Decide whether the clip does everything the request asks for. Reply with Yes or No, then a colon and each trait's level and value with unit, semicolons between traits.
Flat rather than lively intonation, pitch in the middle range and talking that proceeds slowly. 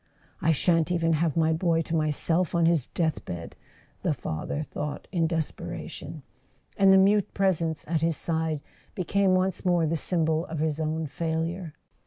No: narrow, 1.8 semitones; medium, 165 Hz; average, 165 wpm